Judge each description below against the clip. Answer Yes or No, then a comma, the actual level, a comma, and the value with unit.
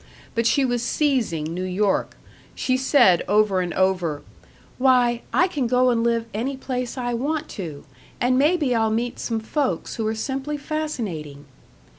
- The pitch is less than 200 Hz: No, high, 240 Hz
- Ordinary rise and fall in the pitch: Yes, average, 4.8 semitones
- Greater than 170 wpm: No, average, 160 wpm